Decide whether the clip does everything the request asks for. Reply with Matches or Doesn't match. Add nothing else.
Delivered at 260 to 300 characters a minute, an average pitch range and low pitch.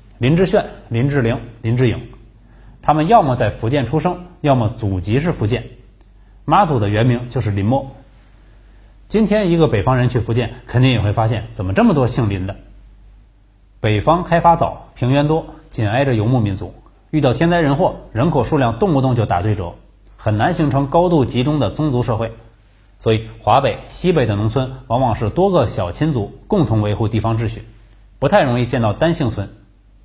Matches